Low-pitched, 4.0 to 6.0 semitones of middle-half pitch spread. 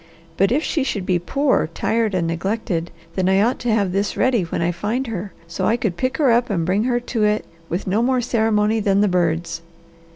No: high, 210 Hz; average, 4.6 semitones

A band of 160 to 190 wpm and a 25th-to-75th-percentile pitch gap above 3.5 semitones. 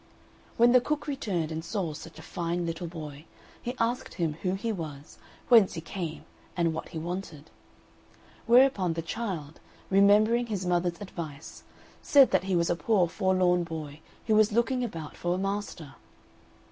Yes: average, 165 wpm; average, 4.7 semitones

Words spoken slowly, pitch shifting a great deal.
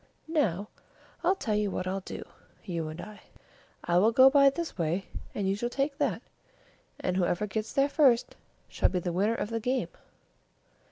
No: average, 180 wpm; wide, 6.0 semitones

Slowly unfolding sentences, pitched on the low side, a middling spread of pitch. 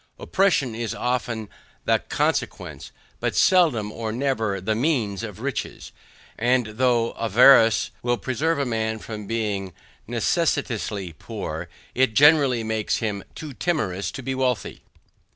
Yes: slow, 130 wpm; low, 115 Hz; average, 3.4 semitones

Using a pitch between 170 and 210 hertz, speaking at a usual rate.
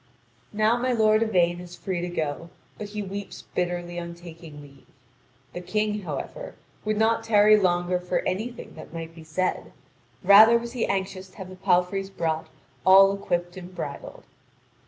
Yes: medium, 185 Hz; average, 165 wpm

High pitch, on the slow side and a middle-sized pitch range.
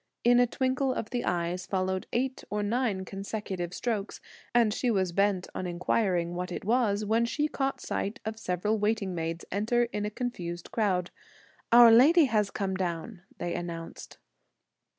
No: high, 205 Hz; average, 165 wpm; average, 4.6 semitones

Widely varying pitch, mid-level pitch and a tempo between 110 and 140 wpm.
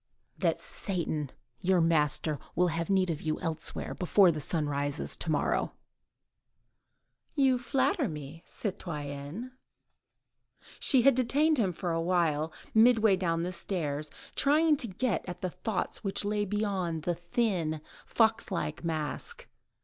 Yes: wide, 5.8 semitones; medium, 180 Hz; slow, 135 wpm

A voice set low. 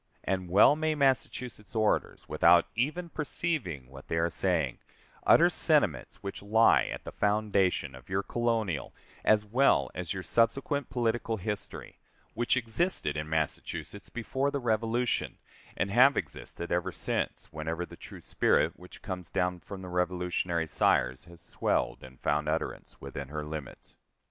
Yes: very low, 95 Hz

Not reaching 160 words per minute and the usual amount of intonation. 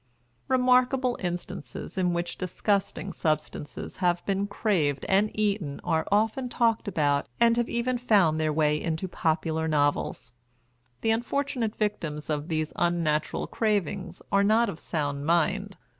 No: slow, 135 wpm; wide, 5.7 semitones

